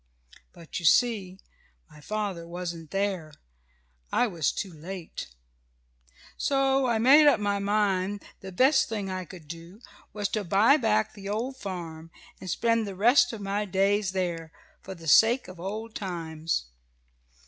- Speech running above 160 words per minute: No, average, 150 wpm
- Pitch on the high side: Yes, high, 195 Hz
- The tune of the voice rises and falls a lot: No, average, 4.0 semitones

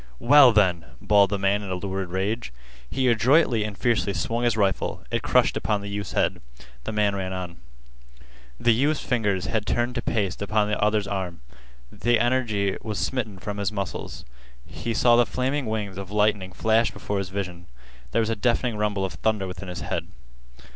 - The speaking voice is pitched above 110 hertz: No, low, 105 Hz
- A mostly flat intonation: No, average, 3.0 semitones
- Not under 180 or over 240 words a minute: Yes, average, 190 wpm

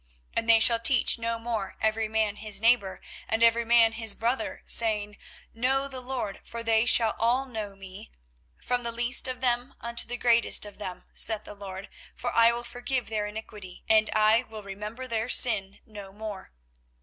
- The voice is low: No, high, 225 Hz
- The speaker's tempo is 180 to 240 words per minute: Yes, average, 185 wpm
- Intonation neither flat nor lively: No, narrow, 2.2 semitones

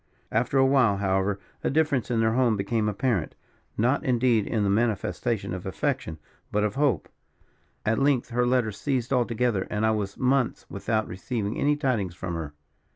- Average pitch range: Yes, average, 4.2 semitones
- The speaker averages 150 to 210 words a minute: Yes, average, 170 wpm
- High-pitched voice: No, low, 115 Hz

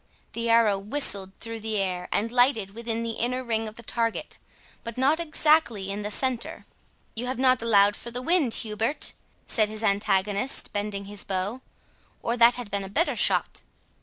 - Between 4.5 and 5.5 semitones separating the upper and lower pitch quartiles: No, average, 3.3 semitones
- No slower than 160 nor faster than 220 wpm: Yes, average, 180 wpm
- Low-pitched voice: No, high, 225 Hz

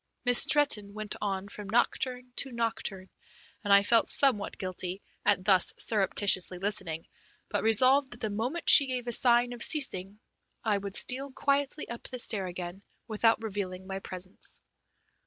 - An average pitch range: Yes, average, 4.2 semitones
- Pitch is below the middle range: No, high, 215 Hz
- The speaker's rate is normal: Yes, average, 155 wpm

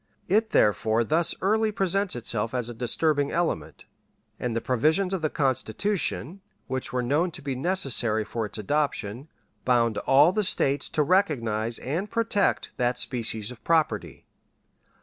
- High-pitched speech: No, medium, 140 Hz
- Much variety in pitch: Yes, wide, 7.0 semitones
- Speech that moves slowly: No, average, 150 wpm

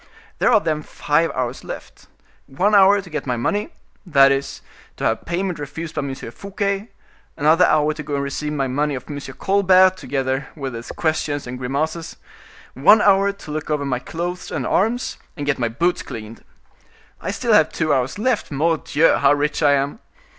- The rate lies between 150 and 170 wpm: No, average, 180 wpm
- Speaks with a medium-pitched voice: Yes, medium, 150 Hz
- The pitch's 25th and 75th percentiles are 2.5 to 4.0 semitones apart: No, average, 4.9 semitones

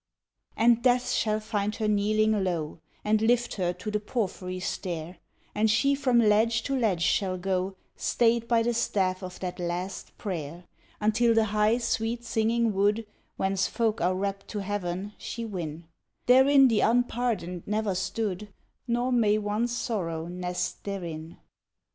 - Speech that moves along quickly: No, average, 150 wpm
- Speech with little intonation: No, average, 3.9 semitones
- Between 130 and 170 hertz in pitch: No, high, 210 Hz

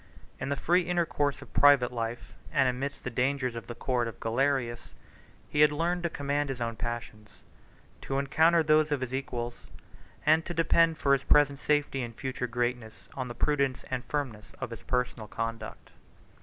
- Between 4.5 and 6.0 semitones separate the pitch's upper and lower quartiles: No, average, 3.6 semitones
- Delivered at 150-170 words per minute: No, average, 180 wpm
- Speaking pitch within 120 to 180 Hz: Yes, low, 135 Hz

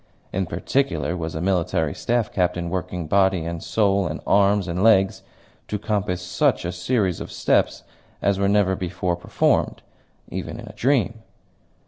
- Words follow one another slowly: No, average, 155 wpm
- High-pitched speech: No, very low, 95 Hz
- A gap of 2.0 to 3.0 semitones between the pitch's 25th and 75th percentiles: Yes, narrow, 2.5 semitones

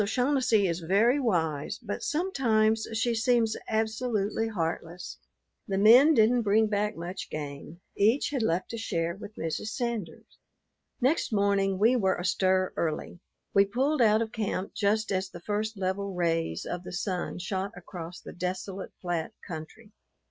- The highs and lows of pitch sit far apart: No, average, 3.8 semitones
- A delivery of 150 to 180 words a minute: Yes, average, 155 wpm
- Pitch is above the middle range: Yes, high, 200 Hz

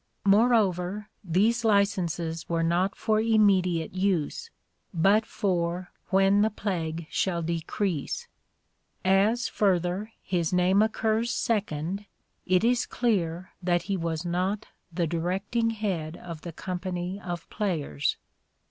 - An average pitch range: Yes, average, 3.4 semitones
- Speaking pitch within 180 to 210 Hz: Yes, medium, 185 Hz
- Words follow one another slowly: Yes, slow, 120 wpm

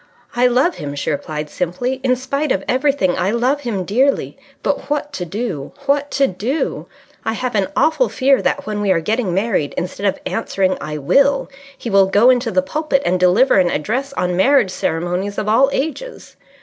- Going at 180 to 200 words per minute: Yes, average, 190 wpm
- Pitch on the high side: Yes, high, 225 Hz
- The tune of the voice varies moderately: No, wide, 6.8 semitones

